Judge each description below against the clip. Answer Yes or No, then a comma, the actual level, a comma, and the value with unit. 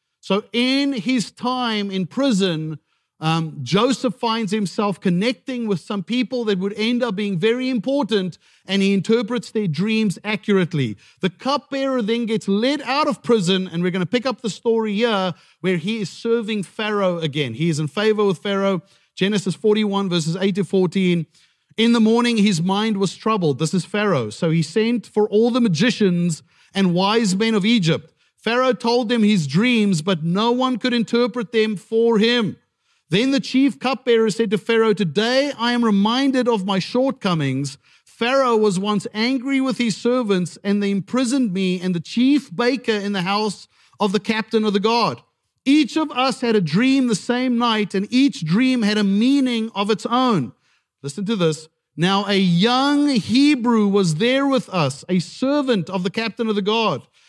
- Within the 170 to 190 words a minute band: Yes, average, 180 wpm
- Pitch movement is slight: No, average, 4.1 semitones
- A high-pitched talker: Yes, high, 215 Hz